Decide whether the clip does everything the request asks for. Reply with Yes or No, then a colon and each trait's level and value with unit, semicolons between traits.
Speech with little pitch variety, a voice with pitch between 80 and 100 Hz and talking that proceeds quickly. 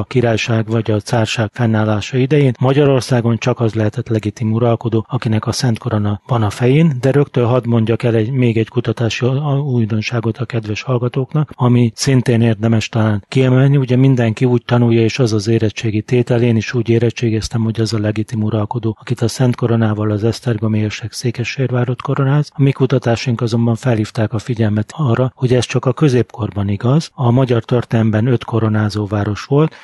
No: narrow, 2.3 semitones; low, 115 Hz; fast, 175 wpm